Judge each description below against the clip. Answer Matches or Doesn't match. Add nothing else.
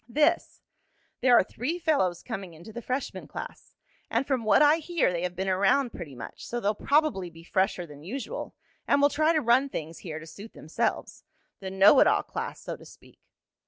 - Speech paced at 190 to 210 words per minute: Matches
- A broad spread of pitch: Matches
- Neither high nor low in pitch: Doesn't match